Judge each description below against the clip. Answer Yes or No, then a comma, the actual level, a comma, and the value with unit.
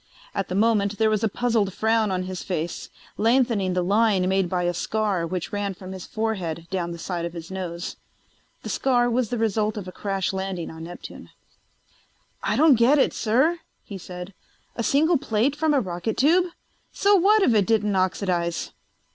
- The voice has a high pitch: Yes, high, 200 Hz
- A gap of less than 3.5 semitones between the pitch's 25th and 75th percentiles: No, average, 4.1 semitones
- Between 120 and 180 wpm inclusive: No, average, 190 wpm